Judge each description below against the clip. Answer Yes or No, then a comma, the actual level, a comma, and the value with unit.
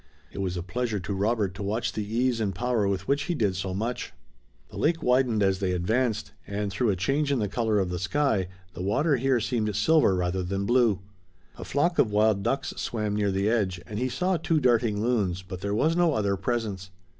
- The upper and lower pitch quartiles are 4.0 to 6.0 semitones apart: Yes, average, 4.3 semitones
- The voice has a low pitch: Yes, low, 105 Hz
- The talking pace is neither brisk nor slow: No, fast, 220 wpm